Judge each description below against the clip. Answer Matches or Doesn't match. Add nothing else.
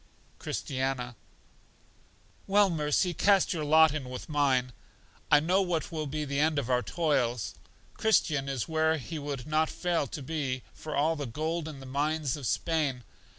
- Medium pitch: Matches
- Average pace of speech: Matches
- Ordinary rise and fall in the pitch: Matches